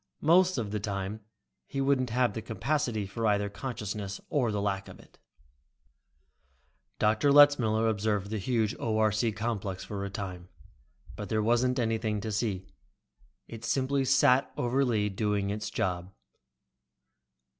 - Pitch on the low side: Yes, low, 110 Hz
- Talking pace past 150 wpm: No, average, 140 wpm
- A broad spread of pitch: No, average, 3.3 semitones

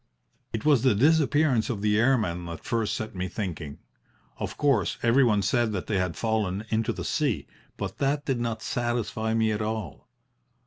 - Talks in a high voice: No, low, 110 Hz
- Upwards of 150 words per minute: Yes, average, 180 wpm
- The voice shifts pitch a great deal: No, average, 3.2 semitones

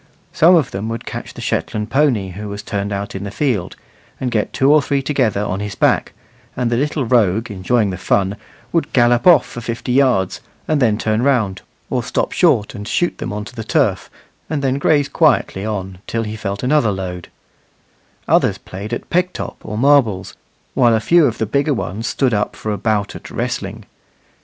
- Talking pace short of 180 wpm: No, average, 200 wpm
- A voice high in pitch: No, low, 115 Hz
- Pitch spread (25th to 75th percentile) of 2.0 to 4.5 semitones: No, average, 4.9 semitones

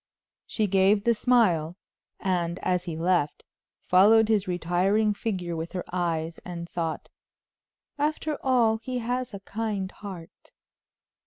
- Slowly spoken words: Yes, slow, 130 wpm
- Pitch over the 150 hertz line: Yes, high, 190 Hz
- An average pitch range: Yes, average, 4.2 semitones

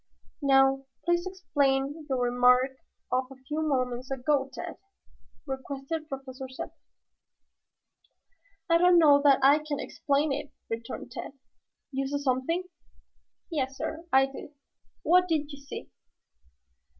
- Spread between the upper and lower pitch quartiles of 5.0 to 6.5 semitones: No, narrow, 2.4 semitones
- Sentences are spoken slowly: Yes, slow, 125 wpm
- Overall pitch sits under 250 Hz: No, very high, 275 Hz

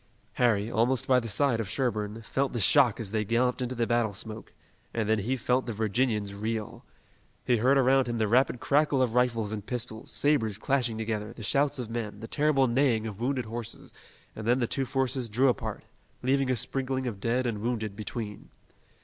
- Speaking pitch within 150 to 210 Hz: No, low, 120 Hz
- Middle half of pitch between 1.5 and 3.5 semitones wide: Yes, average, 2.9 semitones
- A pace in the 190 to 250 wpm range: Yes, average, 200 wpm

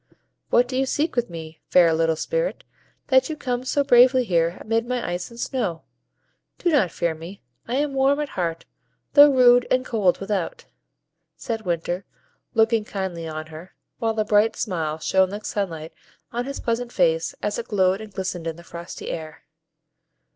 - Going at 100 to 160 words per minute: No, average, 175 wpm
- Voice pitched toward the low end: No, high, 215 Hz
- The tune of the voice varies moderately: No, wide, 6.8 semitones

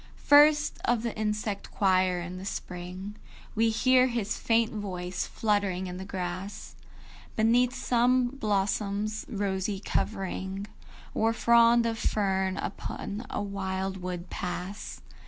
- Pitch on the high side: Yes, high, 205 Hz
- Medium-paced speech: No, slow, 120 wpm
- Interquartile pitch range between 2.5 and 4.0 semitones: Yes, average, 3.2 semitones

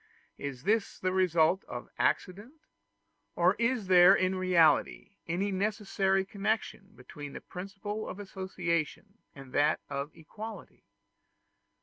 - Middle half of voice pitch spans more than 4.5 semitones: No, average, 3.5 semitones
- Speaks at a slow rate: Yes, slow, 115 wpm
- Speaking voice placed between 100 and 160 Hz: No, medium, 185 Hz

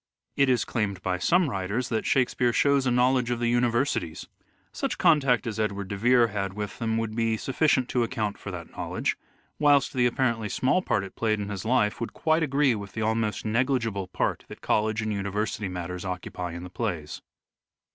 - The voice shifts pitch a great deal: No, average, 3.9 semitones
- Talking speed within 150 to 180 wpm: No, average, 195 wpm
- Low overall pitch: Yes, low, 115 Hz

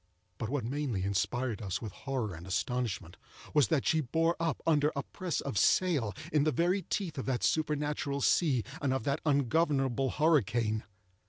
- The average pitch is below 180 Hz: Yes, medium, 140 Hz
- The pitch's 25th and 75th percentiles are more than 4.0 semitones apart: Yes, average, 4.5 semitones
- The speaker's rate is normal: Yes, average, 170 wpm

